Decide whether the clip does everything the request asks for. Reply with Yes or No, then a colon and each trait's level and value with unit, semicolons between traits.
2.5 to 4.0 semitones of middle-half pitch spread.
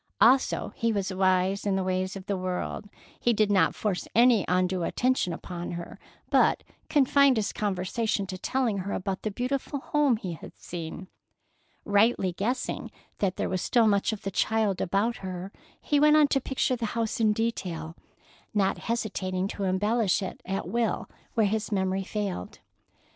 Yes: average, 3.7 semitones